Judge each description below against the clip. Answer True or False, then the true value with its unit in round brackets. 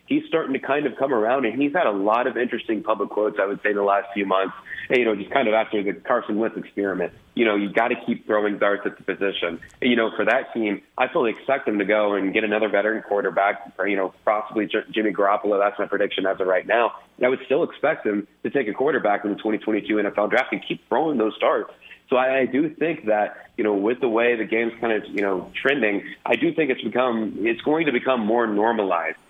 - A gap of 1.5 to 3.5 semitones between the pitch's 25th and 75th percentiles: True (3.2 semitones)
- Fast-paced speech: True (255 wpm)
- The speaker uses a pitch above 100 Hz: True (110 Hz)